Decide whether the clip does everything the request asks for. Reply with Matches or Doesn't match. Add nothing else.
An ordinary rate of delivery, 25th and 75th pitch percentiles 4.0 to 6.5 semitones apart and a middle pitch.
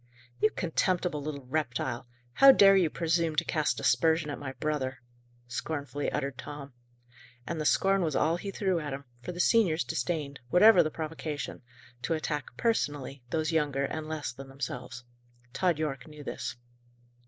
Doesn't match